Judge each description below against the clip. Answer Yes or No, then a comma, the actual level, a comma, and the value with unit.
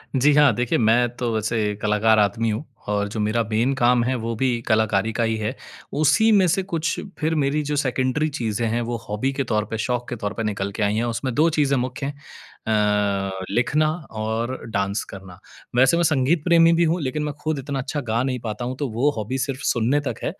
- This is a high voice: No, low, 125 Hz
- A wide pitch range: No, average, 4.7 semitones